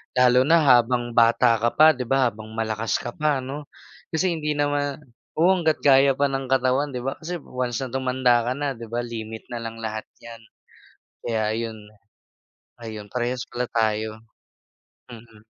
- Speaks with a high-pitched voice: No, low, 125 Hz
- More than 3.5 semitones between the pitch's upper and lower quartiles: No, average, 3.2 semitones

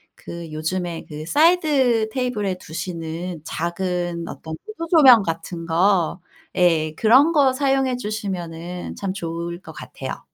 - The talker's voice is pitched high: No, medium, 180 Hz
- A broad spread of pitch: Yes, wide, 6.9 semitones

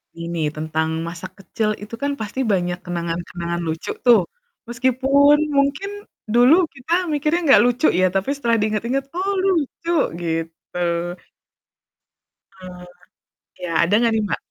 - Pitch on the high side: Yes, high, 220 Hz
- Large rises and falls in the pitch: Yes, wide, 8.3 semitones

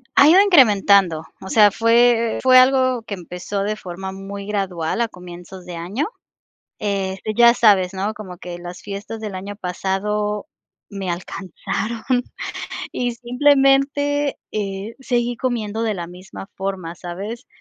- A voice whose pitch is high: Yes, high, 205 Hz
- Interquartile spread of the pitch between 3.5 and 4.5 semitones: Yes, average, 4.0 semitones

